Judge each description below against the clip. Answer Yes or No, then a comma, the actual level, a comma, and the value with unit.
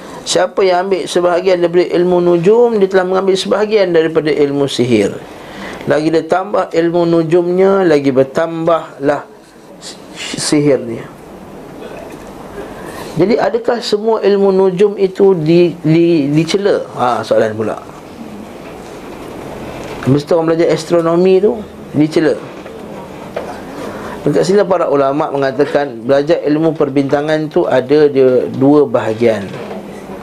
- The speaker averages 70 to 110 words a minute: Yes, average, 105 wpm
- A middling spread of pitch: Yes, average, 4.4 semitones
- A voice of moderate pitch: Yes, medium, 165 Hz